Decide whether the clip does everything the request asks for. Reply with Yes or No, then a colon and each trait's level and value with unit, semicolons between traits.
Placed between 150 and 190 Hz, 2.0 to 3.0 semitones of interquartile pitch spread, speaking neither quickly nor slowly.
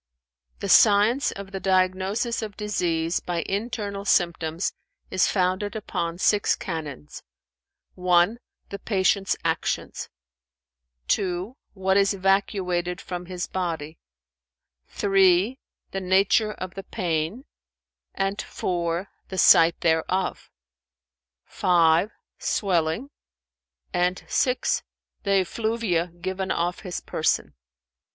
No: medium, 185 Hz; narrow, 2.5 semitones; slow, 100 wpm